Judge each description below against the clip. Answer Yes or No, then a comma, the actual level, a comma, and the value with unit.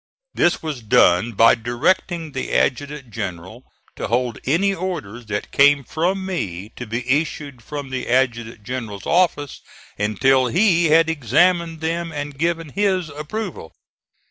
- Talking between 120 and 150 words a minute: Yes, average, 140 wpm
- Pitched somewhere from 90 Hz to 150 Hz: Yes, medium, 140 Hz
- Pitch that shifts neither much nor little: No, wide, 5.8 semitones